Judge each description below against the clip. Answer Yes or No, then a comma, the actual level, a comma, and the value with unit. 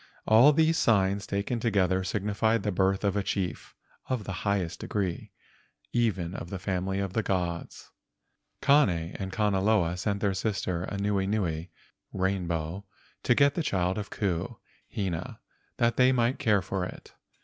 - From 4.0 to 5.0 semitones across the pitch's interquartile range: No, average, 2.8 semitones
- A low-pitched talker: Yes, low, 100 Hz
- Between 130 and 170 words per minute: Yes, average, 150 wpm